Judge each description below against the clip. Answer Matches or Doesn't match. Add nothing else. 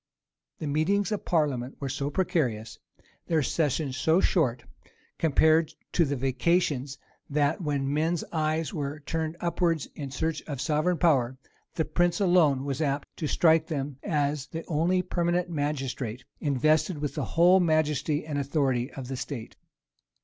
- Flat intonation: Doesn't match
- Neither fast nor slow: Matches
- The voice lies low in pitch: Doesn't match